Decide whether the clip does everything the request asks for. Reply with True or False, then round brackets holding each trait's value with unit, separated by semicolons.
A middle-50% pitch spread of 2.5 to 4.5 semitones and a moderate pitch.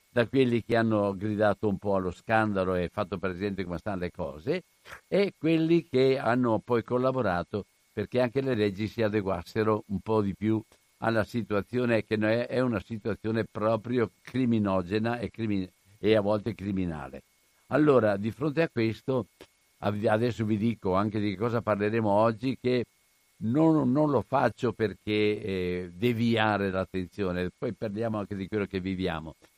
False (3.1 semitones; 110 Hz)